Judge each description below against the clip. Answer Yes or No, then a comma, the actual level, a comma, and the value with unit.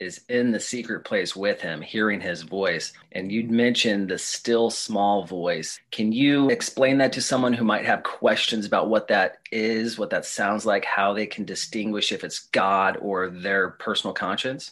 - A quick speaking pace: No, average, 190 wpm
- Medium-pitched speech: No, low, 115 Hz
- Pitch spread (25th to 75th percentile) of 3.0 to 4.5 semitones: No, narrow, 2.6 semitones